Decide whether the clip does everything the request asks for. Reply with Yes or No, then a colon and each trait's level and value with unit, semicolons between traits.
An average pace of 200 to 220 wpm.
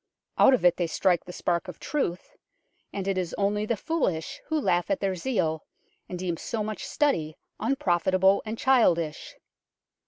No: average, 165 wpm